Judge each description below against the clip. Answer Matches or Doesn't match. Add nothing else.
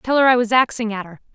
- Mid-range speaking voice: Doesn't match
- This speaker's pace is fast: Matches